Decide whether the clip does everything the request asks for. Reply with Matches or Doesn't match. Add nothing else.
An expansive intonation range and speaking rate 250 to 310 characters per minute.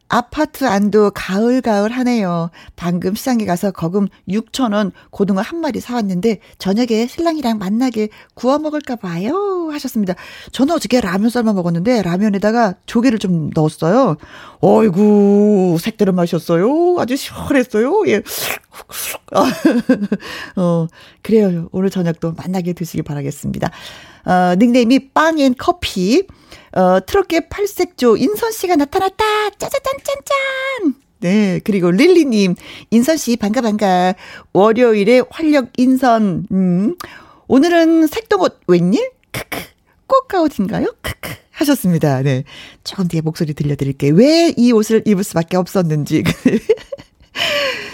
Matches